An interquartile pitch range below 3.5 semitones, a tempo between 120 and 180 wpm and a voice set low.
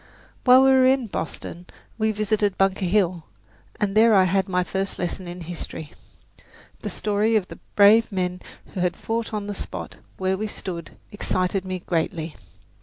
No: average, 2.9 semitones; average, 170 wpm; high, 195 Hz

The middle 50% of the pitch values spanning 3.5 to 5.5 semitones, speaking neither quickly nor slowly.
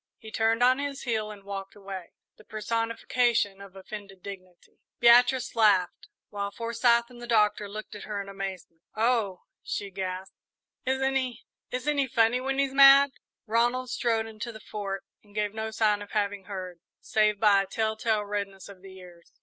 No: average, 3.1 semitones; average, 175 wpm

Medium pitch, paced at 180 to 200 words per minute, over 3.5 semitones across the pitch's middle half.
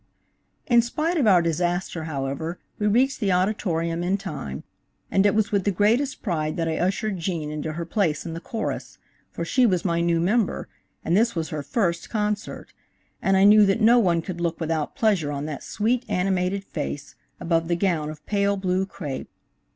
Yes: medium, 180 Hz; average, 190 wpm; average, 4.1 semitones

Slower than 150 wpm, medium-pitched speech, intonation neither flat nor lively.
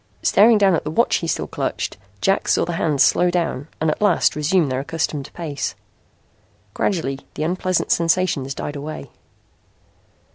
No: average, 155 wpm; medium, 165 Hz; average, 3.9 semitones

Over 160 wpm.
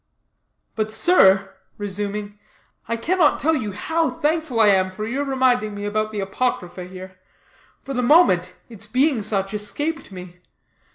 No: average, 150 wpm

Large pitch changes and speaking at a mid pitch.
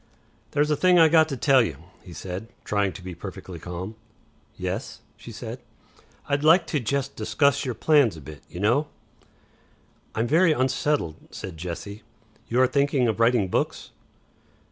No: wide, 7.2 semitones; low, 120 Hz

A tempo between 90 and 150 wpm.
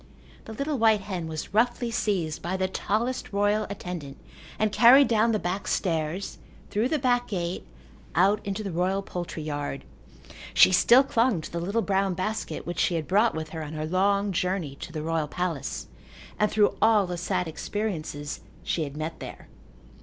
No: average, 180 wpm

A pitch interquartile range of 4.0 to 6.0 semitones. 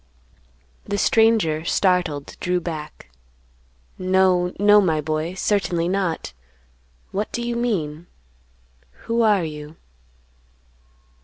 Yes: average, 4.4 semitones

